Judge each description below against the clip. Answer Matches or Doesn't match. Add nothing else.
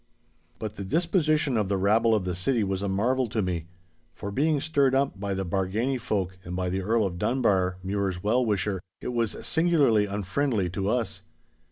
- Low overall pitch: Matches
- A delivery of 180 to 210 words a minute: Matches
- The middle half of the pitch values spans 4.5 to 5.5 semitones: Matches